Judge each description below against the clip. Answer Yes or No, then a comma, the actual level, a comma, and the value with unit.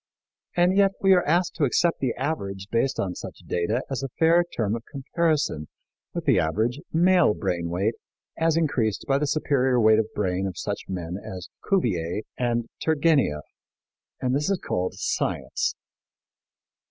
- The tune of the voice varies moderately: No, wide, 8.6 semitones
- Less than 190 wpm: Yes, average, 160 wpm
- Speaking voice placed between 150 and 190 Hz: No, low, 125 Hz